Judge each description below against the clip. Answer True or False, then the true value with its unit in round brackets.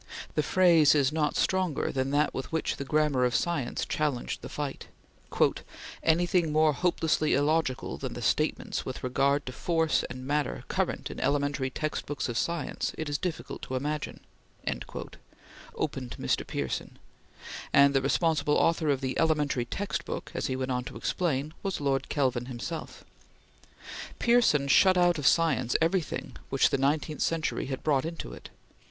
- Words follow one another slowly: False (155 wpm)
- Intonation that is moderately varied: True (3.3 semitones)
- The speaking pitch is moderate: True (150 Hz)